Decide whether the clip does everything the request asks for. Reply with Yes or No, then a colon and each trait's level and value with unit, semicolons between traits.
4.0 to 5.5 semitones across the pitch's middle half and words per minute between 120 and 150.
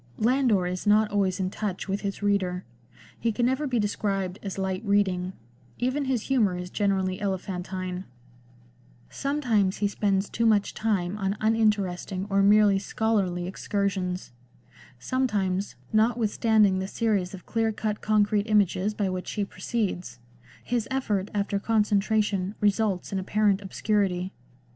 No: narrow, 2.4 semitones; average, 140 wpm